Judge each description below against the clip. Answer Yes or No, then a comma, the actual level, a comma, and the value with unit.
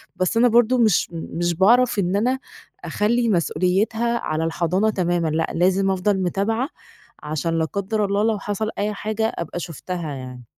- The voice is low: No, high, 195 Hz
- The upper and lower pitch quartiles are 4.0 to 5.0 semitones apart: Yes, average, 4.3 semitones